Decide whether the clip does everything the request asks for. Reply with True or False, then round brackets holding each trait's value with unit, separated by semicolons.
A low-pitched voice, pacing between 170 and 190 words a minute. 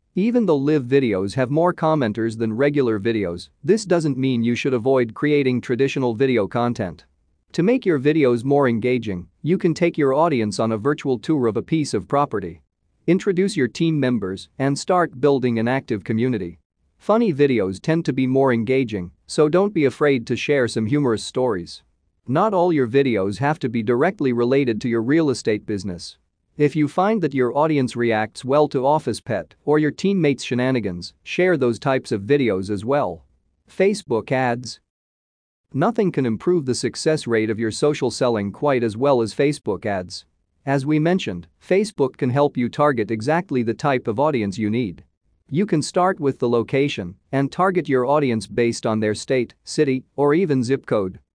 True (130 Hz; 180 wpm)